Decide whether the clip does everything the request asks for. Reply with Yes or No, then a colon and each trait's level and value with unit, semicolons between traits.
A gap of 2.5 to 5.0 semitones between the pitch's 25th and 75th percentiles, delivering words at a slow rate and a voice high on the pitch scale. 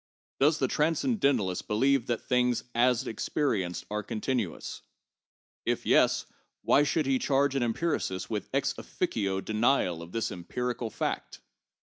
No: average, 4.7 semitones; slow, 130 wpm; low, 125 Hz